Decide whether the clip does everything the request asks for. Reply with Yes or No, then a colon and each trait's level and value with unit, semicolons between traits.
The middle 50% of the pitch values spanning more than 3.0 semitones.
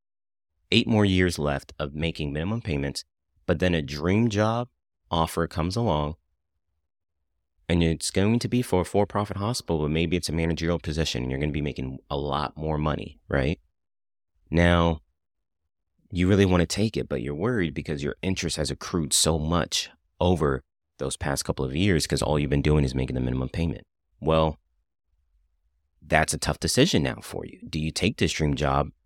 Yes: average, 3.5 semitones